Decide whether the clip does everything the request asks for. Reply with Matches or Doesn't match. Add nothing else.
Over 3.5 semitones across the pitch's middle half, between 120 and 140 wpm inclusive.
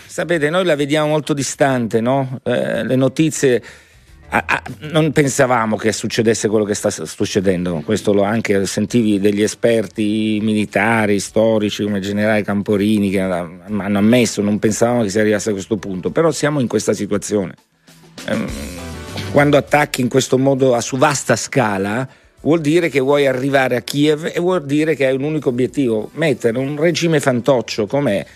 Doesn't match